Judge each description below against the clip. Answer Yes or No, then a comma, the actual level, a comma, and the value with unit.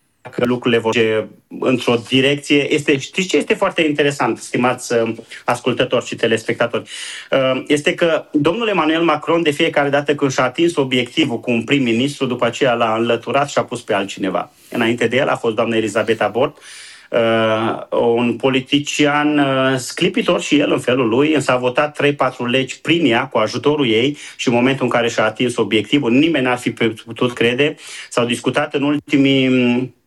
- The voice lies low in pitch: Yes, low, 130 Hz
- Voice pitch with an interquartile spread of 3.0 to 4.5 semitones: Yes, average, 3.6 semitones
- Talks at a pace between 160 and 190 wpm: Yes, average, 165 wpm